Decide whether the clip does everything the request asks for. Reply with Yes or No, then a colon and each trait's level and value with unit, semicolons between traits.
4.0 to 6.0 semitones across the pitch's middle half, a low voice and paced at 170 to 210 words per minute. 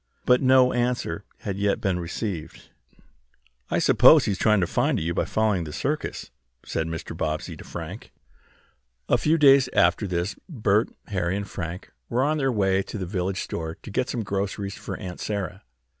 Yes: average, 4.9 semitones; low, 100 Hz; average, 185 wpm